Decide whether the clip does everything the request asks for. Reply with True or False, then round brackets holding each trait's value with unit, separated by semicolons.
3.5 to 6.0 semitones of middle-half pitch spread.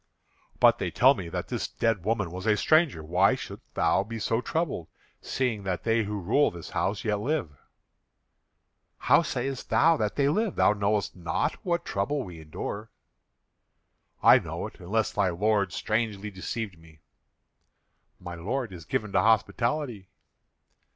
True (4.4 semitones)